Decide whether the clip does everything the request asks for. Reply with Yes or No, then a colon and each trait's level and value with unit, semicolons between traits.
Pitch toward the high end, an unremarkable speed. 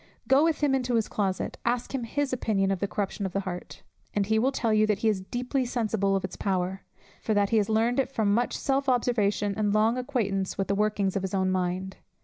No: high, 215 Hz; fast, 240 wpm